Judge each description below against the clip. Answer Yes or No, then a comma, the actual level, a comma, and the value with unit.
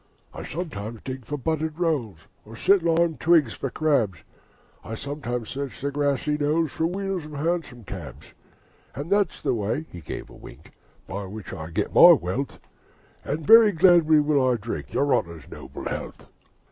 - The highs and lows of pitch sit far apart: Yes, wide, 5.9 semitones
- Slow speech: No, average, 170 wpm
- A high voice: No, medium, 145 Hz